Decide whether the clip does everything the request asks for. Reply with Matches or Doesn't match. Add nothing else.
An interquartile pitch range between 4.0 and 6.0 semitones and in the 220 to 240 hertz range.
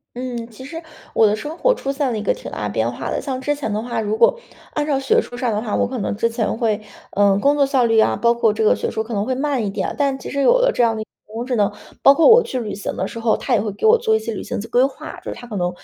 Matches